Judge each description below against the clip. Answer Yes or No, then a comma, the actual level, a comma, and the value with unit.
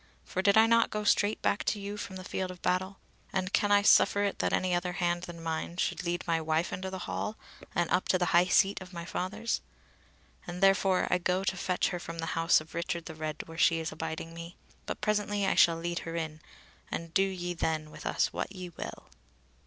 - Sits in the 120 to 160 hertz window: No, medium, 180 Hz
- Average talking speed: No, fast, 230 wpm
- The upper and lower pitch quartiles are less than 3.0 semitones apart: Yes, narrow, 2.6 semitones